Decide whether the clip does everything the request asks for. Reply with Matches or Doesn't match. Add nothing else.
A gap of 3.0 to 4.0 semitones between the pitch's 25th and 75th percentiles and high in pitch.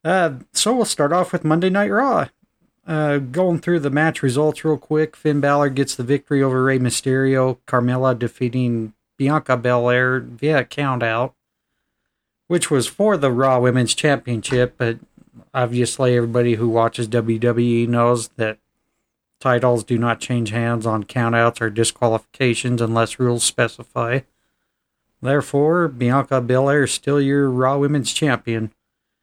Doesn't match